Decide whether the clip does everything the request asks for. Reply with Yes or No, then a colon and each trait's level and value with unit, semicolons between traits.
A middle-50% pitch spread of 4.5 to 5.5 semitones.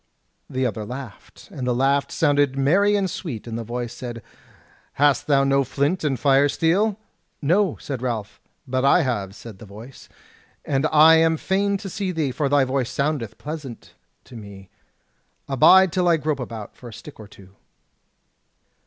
Yes: average, 5.0 semitones